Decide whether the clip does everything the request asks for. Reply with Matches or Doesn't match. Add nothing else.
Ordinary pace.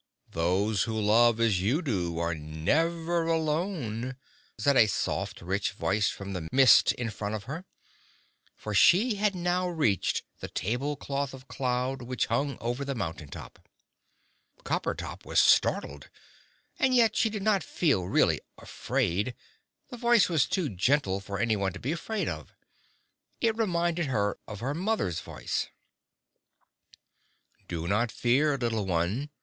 Matches